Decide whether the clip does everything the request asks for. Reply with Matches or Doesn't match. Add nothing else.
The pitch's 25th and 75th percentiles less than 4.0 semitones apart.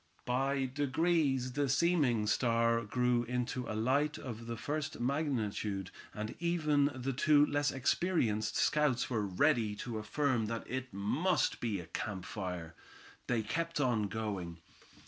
Doesn't match